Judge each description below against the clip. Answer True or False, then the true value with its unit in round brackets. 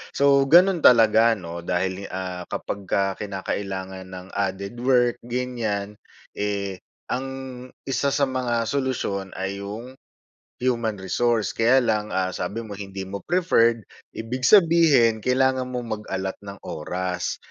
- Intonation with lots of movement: False (4.6 semitones)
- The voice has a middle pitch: False (110 Hz)